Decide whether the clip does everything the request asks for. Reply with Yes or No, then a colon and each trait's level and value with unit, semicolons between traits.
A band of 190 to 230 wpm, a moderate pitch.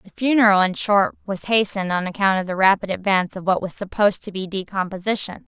No: fast, 205 wpm; high, 195 Hz